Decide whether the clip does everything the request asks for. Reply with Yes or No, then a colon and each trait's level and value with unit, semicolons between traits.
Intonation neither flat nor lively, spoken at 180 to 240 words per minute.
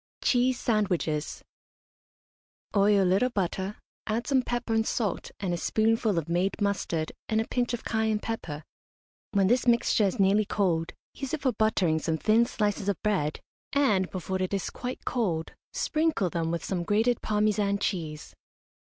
No: average, 3.9 semitones; average, 160 wpm